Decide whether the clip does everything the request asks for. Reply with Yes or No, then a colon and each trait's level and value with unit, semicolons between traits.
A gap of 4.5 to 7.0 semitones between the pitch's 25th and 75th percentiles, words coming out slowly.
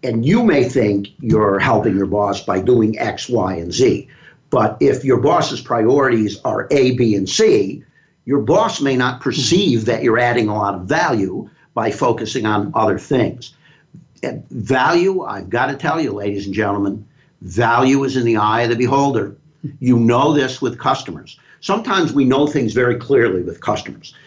No: average, 4.8 semitones; average, 175 wpm